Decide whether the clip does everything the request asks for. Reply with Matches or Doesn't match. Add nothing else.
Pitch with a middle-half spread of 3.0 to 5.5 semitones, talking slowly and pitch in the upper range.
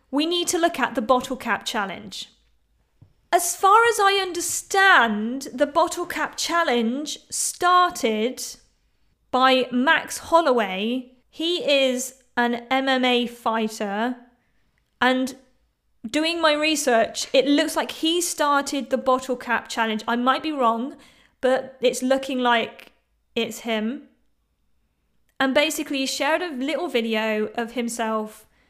Matches